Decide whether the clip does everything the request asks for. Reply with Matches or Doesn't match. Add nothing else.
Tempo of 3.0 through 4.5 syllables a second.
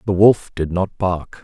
Matches